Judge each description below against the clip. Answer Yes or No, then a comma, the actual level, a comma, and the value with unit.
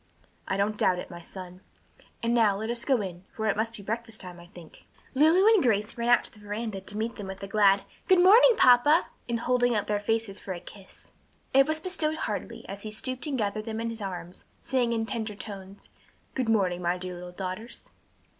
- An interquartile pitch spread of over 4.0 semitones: No, average, 3.7 semitones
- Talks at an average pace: No, fast, 220 wpm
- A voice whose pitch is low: No, high, 215 Hz